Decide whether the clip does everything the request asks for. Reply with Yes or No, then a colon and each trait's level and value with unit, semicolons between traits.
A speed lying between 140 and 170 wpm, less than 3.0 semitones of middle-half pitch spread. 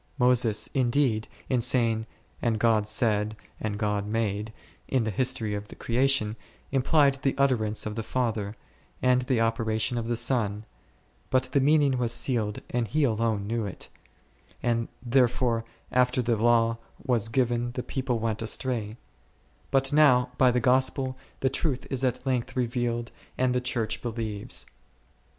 Yes: average, 155 wpm; narrow, 2.6 semitones